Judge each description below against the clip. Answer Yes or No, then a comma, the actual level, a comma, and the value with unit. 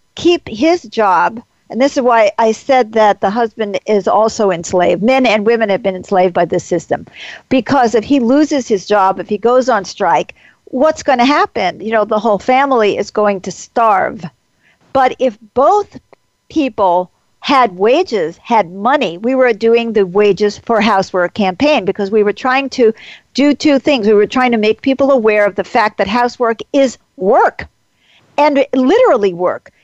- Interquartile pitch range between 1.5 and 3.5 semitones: No, average, 4.5 semitones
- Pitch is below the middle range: No, high, 230 Hz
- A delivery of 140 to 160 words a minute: No, average, 180 wpm